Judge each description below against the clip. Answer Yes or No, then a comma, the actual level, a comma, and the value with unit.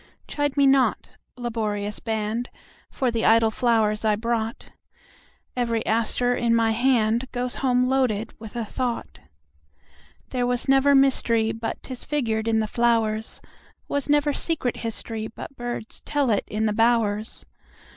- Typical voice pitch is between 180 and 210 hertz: No, high, 230 Hz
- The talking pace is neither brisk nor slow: No, slow, 120 wpm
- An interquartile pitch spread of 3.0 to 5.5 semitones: No, narrow, 2.4 semitones